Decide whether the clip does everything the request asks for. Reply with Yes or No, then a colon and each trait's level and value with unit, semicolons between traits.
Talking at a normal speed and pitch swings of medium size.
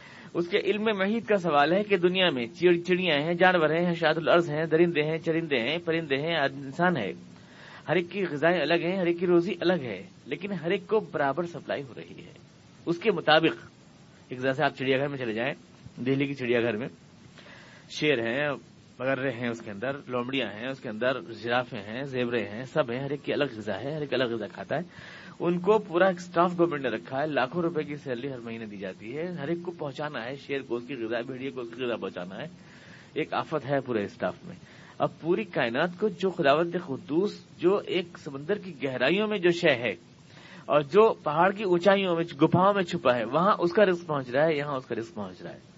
No: fast, 225 wpm; average, 4.9 semitones